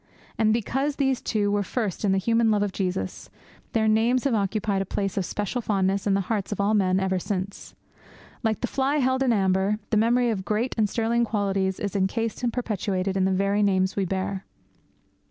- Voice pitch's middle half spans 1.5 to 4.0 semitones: Yes, average, 2.9 semitones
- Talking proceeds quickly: Yes, fast, 210 wpm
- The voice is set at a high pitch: Yes, high, 205 Hz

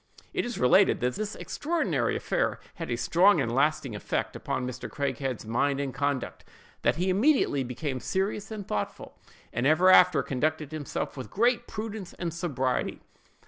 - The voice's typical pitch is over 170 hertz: No, medium, 155 Hz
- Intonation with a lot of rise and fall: Yes, wide, 6.9 semitones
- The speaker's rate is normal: Yes, average, 160 wpm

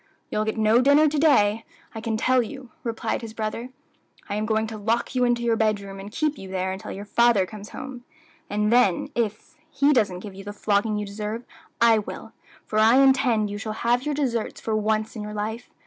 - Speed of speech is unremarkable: No, fast, 215 wpm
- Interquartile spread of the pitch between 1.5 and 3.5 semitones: Yes, narrow, 2.5 semitones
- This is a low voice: No, high, 220 Hz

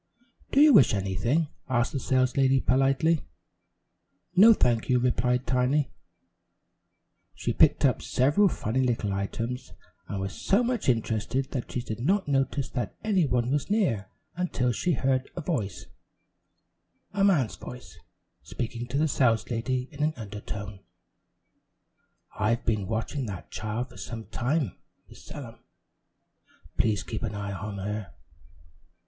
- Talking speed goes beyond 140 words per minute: No, slow, 135 wpm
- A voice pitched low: Yes, low, 125 Hz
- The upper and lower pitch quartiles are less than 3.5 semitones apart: No, average, 4.3 semitones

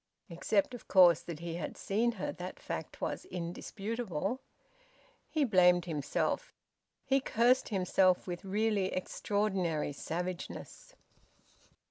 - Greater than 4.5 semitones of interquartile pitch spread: No, average, 4.1 semitones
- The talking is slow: Yes, slow, 110 wpm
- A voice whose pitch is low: No, high, 190 Hz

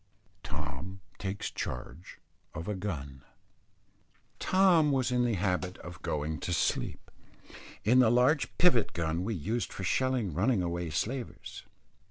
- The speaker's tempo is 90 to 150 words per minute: Yes, slow, 135 wpm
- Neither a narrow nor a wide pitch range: No, wide, 6.7 semitones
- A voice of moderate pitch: No, very low, 95 Hz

